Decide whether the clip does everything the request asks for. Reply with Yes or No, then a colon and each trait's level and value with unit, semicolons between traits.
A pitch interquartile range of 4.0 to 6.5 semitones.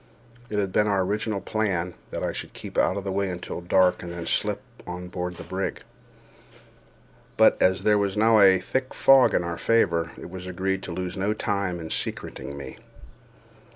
No: narrow, 2.4 semitones